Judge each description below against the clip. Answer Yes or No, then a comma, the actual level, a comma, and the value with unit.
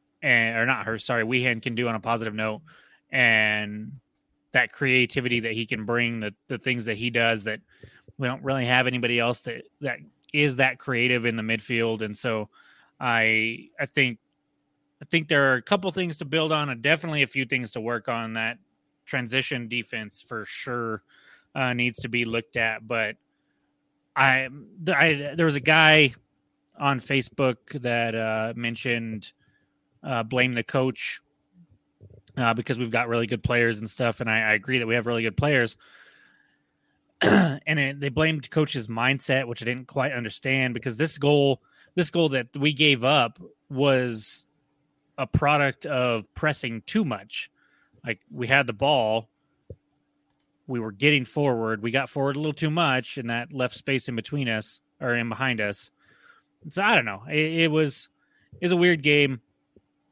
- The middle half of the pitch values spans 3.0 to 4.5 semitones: Yes, average, 3.6 semitones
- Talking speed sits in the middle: Yes, average, 175 wpm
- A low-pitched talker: Yes, low, 125 Hz